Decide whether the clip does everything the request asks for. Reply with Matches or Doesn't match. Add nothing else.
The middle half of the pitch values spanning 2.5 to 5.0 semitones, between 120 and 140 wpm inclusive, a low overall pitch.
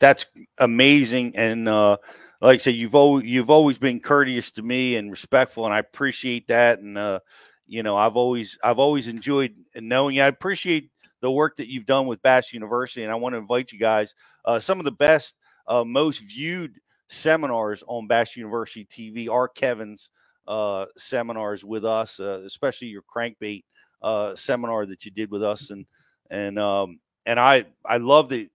Doesn't match